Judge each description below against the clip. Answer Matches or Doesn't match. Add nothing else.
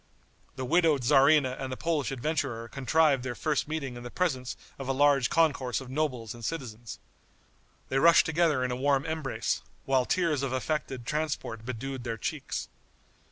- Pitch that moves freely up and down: Doesn't match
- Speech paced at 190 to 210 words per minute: Doesn't match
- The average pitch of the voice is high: Doesn't match